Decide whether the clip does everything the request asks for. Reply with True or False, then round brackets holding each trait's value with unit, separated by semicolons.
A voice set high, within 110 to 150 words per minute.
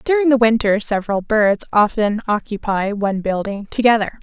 True (215 Hz; 140 wpm)